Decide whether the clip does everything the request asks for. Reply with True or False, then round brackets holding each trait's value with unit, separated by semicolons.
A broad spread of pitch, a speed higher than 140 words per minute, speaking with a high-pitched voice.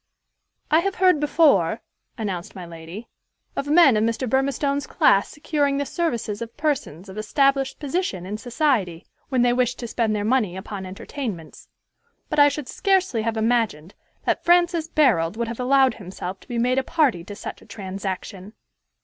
True (6.1 semitones; 170 wpm; 240 Hz)